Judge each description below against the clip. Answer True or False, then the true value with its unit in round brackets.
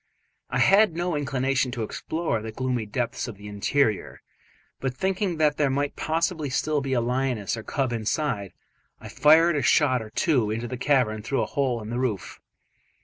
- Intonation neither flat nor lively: True (4.5 semitones)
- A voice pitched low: True (130 Hz)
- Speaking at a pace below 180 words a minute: False (185 wpm)